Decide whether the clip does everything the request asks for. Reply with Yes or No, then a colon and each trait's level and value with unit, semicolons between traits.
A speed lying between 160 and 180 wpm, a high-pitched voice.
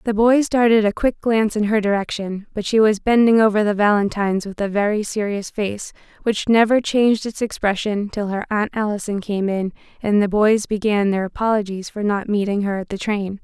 No: average, 200 wpm; high, 210 Hz